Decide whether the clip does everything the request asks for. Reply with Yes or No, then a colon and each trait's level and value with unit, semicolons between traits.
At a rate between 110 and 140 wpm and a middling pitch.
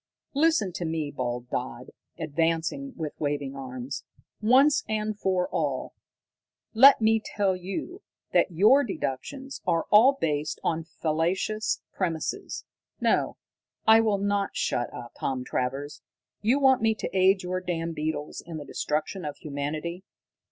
Yes: slow, 135 wpm; medium, 175 Hz